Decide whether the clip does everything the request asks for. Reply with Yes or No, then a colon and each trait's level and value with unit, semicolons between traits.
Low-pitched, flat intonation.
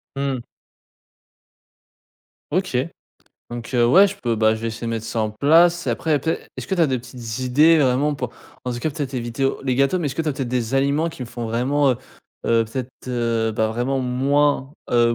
No: low, 130 Hz; average, 3.5 semitones